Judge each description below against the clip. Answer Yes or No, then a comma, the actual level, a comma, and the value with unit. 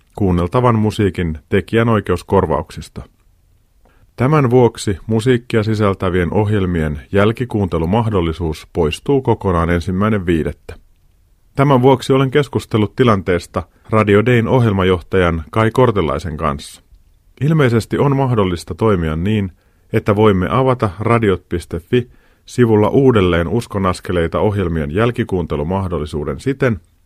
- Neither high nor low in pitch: No, low, 100 Hz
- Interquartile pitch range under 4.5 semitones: No, average, 4.9 semitones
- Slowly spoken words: Yes, slow, 85 wpm